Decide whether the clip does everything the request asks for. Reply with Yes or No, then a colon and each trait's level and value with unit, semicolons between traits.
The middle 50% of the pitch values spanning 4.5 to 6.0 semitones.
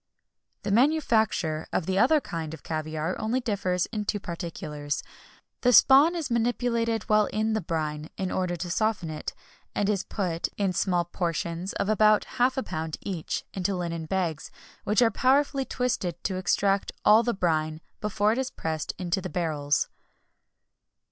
Yes: average, 5.1 semitones